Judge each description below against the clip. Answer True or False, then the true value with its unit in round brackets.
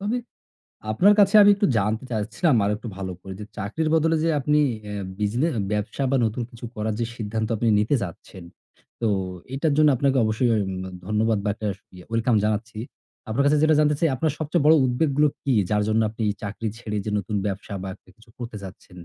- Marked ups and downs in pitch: True (5.9 semitones)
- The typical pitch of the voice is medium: False (115 Hz)